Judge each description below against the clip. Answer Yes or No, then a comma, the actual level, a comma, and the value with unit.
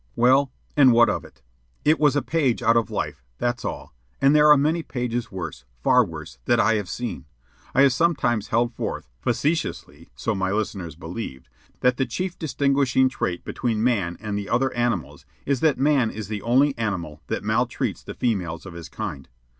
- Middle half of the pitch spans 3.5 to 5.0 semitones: No, wide, 5.4 semitones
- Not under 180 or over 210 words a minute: Yes, average, 185 wpm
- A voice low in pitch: Yes, low, 120 Hz